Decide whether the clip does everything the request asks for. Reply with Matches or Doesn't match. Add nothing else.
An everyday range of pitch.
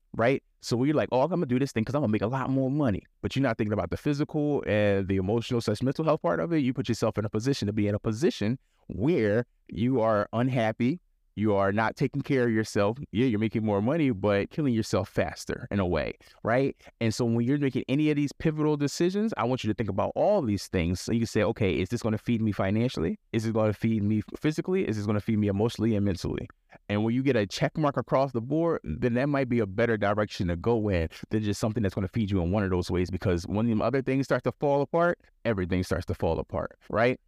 Matches